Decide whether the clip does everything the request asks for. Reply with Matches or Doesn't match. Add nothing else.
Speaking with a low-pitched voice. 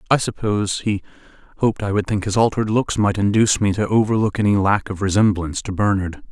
Matches